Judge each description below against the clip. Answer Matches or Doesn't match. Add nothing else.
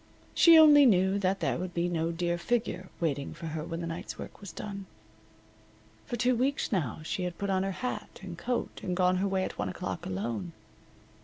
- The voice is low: Doesn't match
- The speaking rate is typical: Doesn't match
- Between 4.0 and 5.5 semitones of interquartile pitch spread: Doesn't match